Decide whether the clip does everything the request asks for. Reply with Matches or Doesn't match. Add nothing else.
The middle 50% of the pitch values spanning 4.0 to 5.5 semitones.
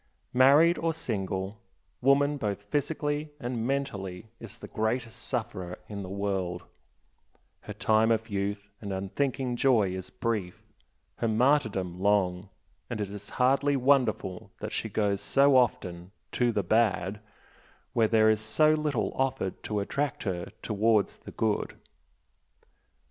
Matches